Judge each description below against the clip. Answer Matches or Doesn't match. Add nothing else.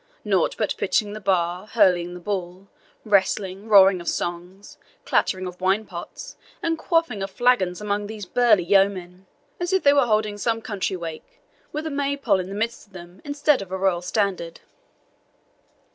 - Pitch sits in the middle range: Doesn't match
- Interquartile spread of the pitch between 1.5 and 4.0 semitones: Matches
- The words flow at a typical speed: Matches